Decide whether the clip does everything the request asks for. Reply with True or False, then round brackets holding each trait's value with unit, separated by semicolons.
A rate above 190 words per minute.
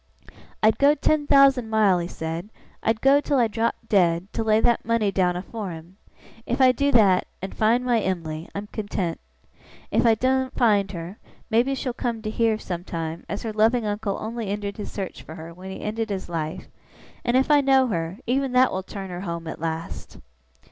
True (200 wpm)